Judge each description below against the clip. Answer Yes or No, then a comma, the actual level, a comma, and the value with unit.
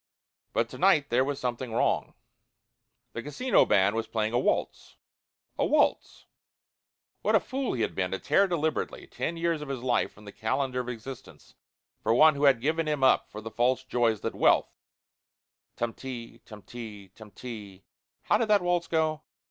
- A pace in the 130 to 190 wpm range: Yes, average, 180 wpm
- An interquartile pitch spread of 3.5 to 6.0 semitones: Yes, wide, 5.4 semitones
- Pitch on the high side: No, low, 125 Hz